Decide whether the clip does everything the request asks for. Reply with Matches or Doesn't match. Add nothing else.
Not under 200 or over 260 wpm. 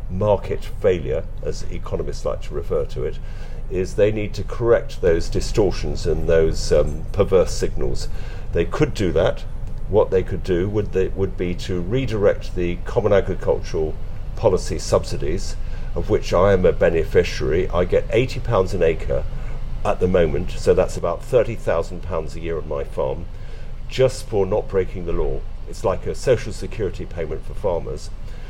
Doesn't match